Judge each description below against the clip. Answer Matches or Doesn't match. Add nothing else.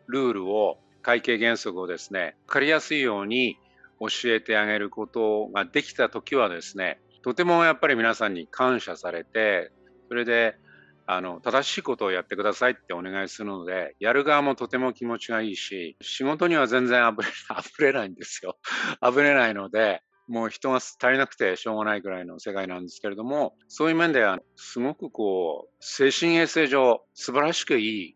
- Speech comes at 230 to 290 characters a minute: Doesn't match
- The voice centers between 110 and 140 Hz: Matches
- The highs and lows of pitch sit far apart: Doesn't match